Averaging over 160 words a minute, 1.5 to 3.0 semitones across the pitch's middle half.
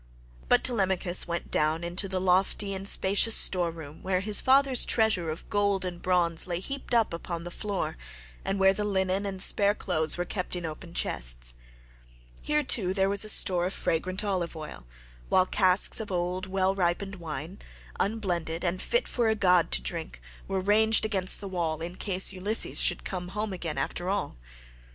Yes: average, 185 wpm; average, 2.7 semitones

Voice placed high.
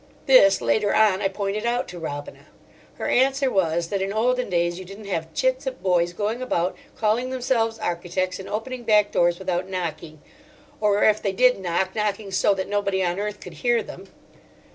Yes: high, 200 Hz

